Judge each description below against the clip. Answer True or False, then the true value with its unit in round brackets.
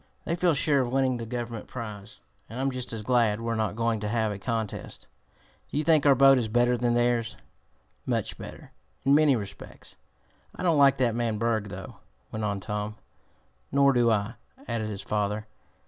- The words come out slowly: False (190 wpm)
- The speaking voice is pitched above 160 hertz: False (115 Hz)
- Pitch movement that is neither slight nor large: True (3.5 semitones)